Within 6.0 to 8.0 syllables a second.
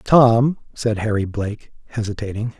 No: 4.6 syllables/s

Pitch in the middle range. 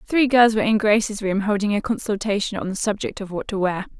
No: high, 210 Hz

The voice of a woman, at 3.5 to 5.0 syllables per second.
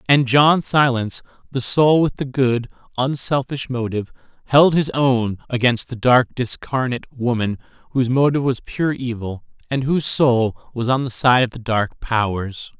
No: male; 4.7 syllables/s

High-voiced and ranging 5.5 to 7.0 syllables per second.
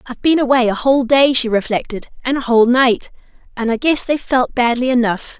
Yes: very high, 250 Hz; 6.0 syllables/s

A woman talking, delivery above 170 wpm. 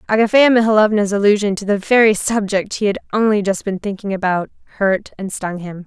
Yes: female; average, 185 wpm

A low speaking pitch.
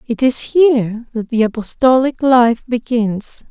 No: high, 240 Hz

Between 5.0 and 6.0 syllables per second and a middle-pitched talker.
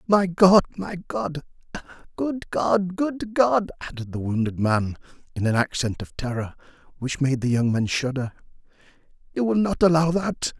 No: 4.6 syllables/s; medium, 155 Hz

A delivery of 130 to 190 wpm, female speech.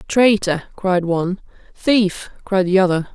Yes: slow, 135 wpm; female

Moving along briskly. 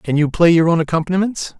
Yes: fast, 225 wpm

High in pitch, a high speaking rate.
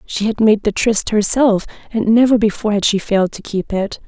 Yes: high, 210 Hz; fast, 220 wpm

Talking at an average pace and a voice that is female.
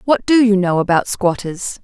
Yes: average, 195 wpm; female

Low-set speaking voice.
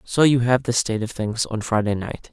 Yes: low, 115 Hz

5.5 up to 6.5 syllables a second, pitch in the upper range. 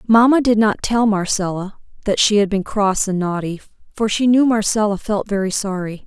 No: 5.1 syllables/s; high, 205 Hz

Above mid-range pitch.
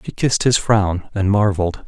No: low, 100 Hz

